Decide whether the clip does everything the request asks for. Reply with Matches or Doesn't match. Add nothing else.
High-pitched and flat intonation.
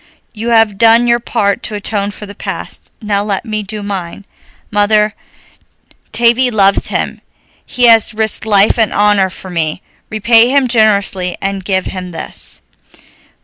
Matches